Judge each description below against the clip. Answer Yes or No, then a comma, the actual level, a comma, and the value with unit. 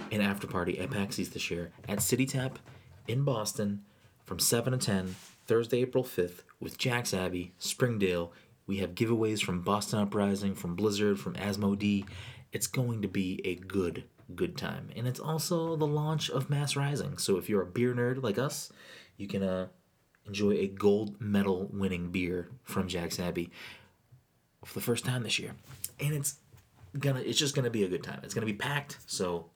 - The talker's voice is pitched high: No, low, 105 Hz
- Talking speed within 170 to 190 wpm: Yes, average, 185 wpm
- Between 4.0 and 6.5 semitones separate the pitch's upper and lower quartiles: Yes, average, 4.7 semitones